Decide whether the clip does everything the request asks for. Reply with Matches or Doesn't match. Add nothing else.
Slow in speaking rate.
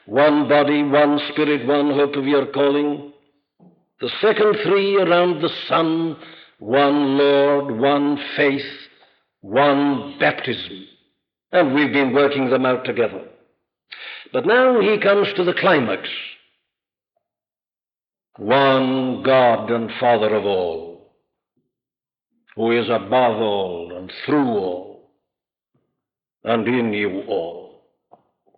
Matches